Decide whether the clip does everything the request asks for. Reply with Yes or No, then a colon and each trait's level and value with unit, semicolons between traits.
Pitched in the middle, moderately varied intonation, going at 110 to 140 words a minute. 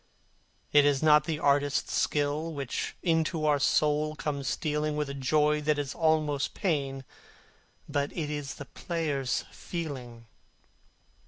No: medium, 150 Hz; narrow, 1.5 semitones; slow, 135 wpm